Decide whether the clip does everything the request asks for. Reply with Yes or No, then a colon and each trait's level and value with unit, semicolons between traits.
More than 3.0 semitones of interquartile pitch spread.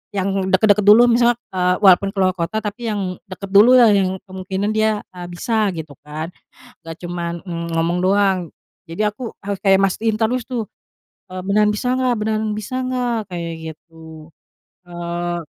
Yes: average, 3.7 semitones